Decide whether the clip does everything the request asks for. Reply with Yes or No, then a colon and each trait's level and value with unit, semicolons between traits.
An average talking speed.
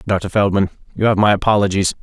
Yes: average, 180 wpm